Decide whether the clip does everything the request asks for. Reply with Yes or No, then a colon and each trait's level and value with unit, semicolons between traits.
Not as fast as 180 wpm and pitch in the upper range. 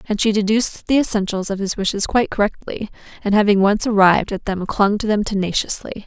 No: average, 200 wpm; high, 205 Hz